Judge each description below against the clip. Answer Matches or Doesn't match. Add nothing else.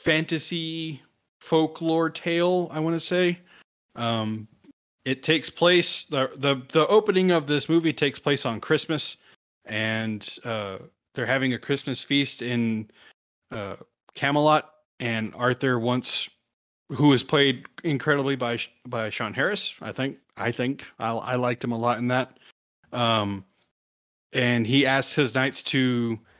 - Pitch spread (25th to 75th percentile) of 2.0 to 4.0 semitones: Doesn't match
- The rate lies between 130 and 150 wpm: Matches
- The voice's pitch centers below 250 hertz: Matches